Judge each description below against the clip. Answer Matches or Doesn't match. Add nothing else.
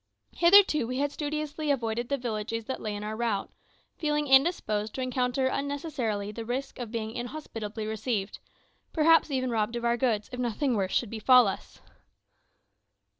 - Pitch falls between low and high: Doesn't match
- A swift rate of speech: Doesn't match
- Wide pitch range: Doesn't match